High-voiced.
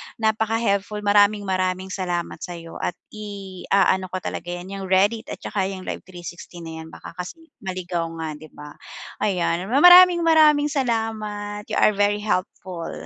Yes: high, 195 Hz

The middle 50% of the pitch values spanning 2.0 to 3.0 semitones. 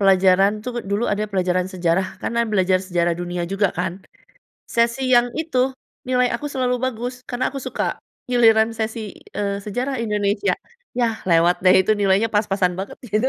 No: average, 4.1 semitones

